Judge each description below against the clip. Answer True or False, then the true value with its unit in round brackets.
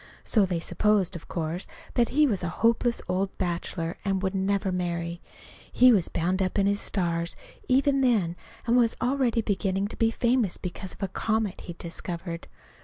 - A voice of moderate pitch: False (195 Hz)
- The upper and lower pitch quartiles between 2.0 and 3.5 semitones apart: False (4.6 semitones)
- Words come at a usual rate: True (180 wpm)